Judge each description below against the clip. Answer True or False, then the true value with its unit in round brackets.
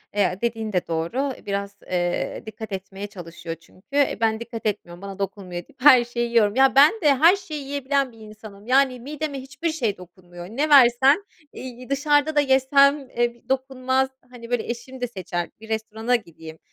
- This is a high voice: True (235 Hz)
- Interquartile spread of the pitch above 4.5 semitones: True (5.2 semitones)